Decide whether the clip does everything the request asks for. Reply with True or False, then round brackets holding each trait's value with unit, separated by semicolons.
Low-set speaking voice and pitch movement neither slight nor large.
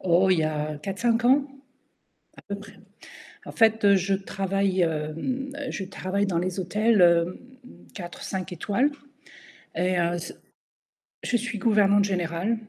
False (195 Hz; 3.2 semitones)